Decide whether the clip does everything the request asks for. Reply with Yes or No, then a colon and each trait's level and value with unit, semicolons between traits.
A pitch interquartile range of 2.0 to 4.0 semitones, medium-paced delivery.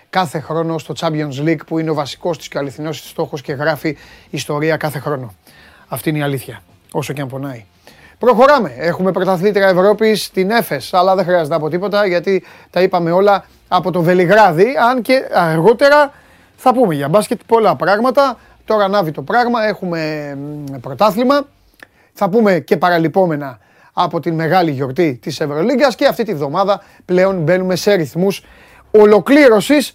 No: average, 5.2 semitones; average, 160 wpm